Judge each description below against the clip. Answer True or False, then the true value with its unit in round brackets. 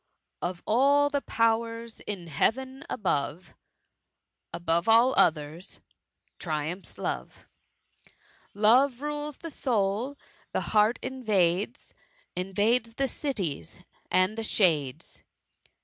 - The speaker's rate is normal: False (100 wpm)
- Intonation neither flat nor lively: False (6.5 semitones)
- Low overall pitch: False (215 Hz)